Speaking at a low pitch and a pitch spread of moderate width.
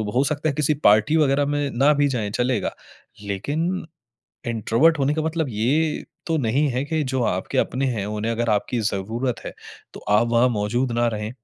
Yes: low, 125 Hz; average, 4.6 semitones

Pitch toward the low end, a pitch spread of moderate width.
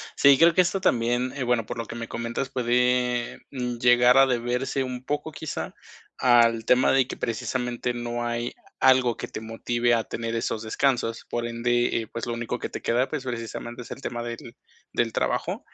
No: low, 120 Hz; narrow, 1.4 semitones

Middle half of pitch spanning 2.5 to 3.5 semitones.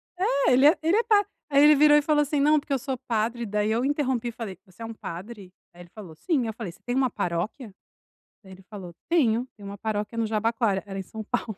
No: average, 5.3 semitones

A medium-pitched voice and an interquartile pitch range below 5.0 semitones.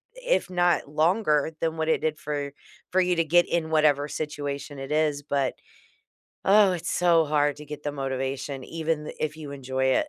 Yes: medium, 150 Hz; narrow, 2.5 semitones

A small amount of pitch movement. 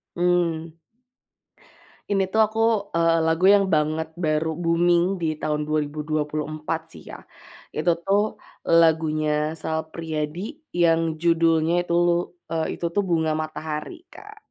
Yes: narrow, 1.7 semitones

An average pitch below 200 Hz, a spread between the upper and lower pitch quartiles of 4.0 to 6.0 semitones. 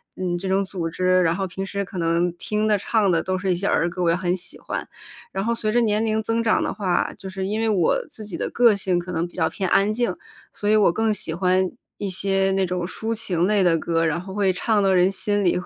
No: high, 190 Hz; average, 2.8 semitones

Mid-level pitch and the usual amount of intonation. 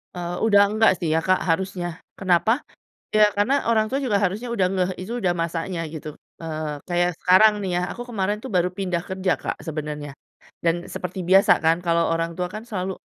Yes: medium, 180 Hz; average, 3.4 semitones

